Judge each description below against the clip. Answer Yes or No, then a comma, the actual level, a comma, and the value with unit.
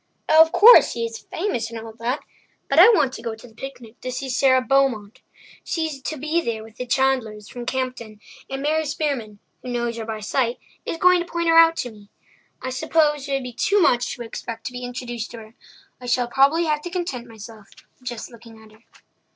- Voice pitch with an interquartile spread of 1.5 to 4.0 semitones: No, average, 4.5 semitones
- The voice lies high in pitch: Yes, very high, 250 Hz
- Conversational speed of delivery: No, fast, 225 wpm